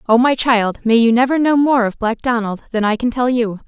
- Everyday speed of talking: No, fast, 260 wpm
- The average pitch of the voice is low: No, high, 235 Hz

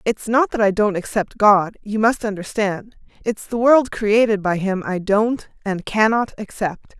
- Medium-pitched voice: No, high, 210 Hz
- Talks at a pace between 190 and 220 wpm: No, average, 180 wpm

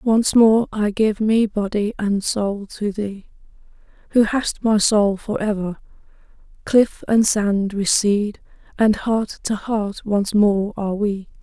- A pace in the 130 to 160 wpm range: Yes, average, 145 wpm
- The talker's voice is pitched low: No, high, 210 Hz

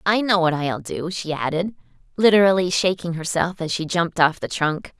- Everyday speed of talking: Yes, average, 190 wpm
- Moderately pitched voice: Yes, medium, 175 Hz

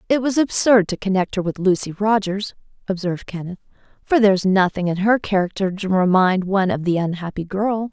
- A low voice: No, high, 195 Hz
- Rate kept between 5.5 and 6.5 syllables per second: Yes, 5.8 syllables/s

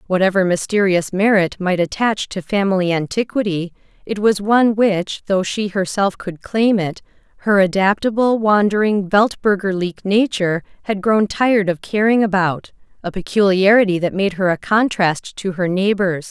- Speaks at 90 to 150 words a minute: Yes, average, 140 wpm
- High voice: Yes, high, 195 Hz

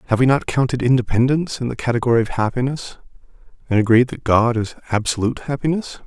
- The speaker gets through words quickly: No, average, 170 wpm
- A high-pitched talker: No, low, 125 Hz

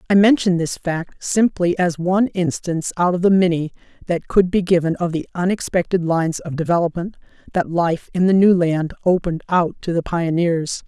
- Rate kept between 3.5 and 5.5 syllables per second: Yes, 5.2 syllables/s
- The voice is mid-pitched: Yes, medium, 175 Hz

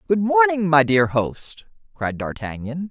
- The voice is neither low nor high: Yes, medium, 150 Hz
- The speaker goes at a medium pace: Yes, average, 145 wpm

